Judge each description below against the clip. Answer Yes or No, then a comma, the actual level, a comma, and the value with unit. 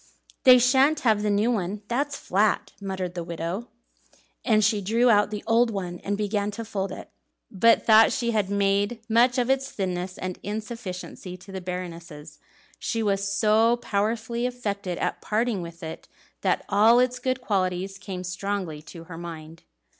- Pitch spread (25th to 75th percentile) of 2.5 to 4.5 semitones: Yes, average, 3.9 semitones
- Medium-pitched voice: No, high, 205 Hz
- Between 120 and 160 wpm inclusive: No, average, 170 wpm